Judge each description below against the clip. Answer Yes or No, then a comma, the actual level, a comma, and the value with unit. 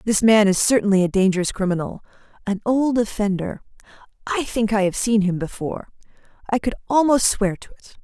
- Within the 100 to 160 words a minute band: Yes, average, 150 wpm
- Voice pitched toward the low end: No, high, 210 Hz